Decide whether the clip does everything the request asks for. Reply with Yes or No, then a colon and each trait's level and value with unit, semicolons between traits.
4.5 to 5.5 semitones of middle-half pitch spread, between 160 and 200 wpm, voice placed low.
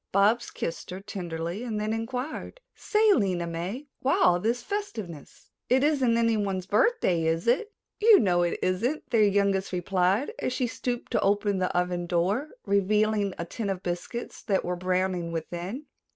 No: average, 5.0 semitones; average, 165 wpm; high, 200 Hz